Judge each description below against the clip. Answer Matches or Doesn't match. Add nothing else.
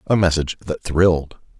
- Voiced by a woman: Doesn't match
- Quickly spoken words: Doesn't match